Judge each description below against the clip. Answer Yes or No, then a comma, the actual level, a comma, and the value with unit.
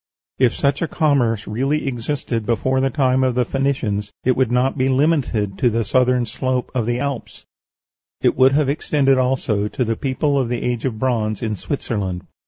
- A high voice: No, low, 125 Hz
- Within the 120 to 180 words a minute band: No, average, 190 wpm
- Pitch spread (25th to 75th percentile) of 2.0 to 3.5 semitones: Yes, average, 3.0 semitones